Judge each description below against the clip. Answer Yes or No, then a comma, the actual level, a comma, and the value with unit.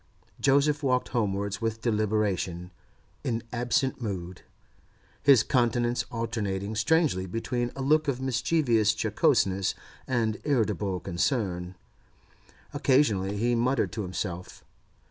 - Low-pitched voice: Yes, low, 115 Hz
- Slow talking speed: Yes, slow, 105 wpm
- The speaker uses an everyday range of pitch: Yes, average, 4.5 semitones